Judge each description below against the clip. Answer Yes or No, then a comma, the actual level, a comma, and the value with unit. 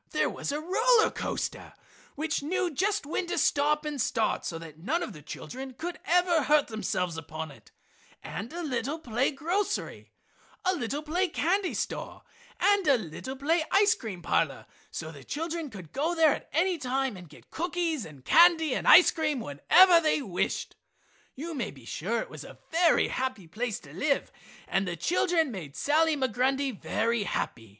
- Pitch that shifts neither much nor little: No, wide, 7.6 semitones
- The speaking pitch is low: No, very high, 285 Hz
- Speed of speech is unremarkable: Yes, average, 180 wpm